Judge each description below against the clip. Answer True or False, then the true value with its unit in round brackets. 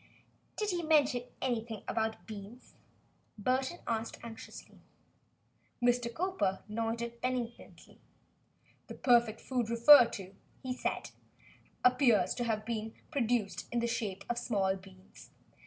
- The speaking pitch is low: False (235 Hz)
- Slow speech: True (120 wpm)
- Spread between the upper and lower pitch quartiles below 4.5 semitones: True (2.4 semitones)